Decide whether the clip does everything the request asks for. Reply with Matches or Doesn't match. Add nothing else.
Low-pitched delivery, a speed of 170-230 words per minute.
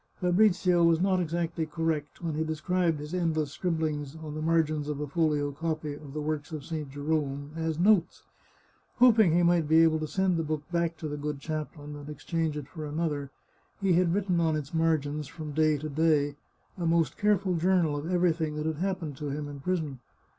Doesn't match